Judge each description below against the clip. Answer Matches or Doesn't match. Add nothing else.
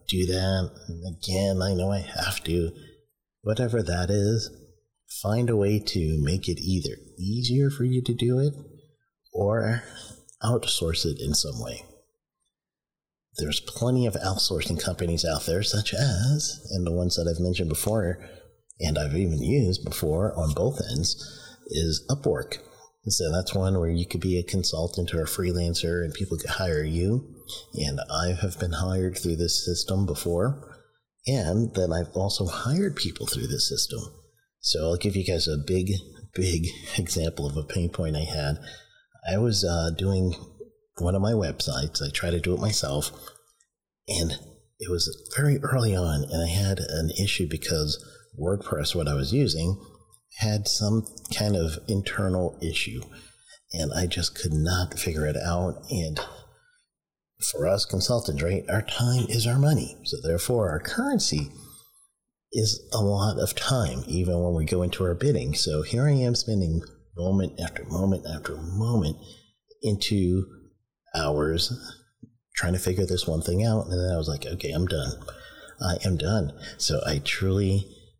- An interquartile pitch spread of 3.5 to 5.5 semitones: Matches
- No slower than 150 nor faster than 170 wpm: Matches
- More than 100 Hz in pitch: Doesn't match